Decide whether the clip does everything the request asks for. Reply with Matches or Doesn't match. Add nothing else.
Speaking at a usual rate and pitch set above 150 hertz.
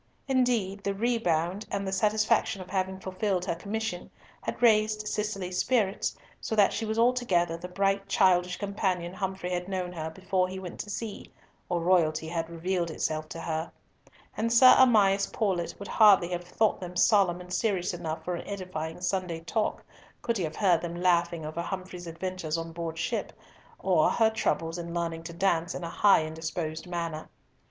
Matches